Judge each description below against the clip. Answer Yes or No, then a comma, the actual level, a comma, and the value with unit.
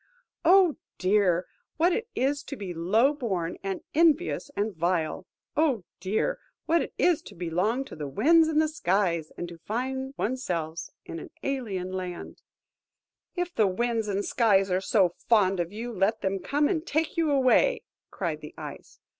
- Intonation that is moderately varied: No, wide, 7.9 semitones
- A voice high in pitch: Yes, high, 220 Hz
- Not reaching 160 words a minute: No, average, 175 wpm